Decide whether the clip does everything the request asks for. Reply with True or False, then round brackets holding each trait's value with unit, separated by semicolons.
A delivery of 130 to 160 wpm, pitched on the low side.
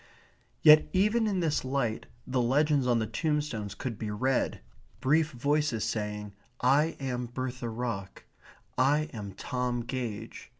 True (135 wpm; 130 Hz)